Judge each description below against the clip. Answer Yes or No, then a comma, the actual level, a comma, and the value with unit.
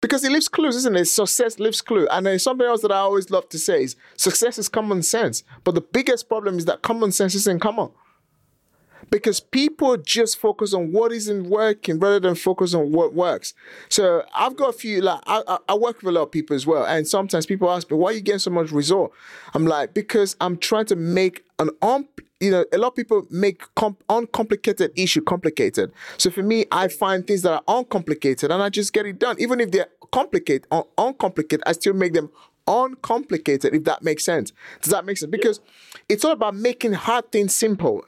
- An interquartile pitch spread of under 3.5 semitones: No, average, 4.5 semitones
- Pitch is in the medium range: No, high, 205 Hz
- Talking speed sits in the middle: No, fast, 215 wpm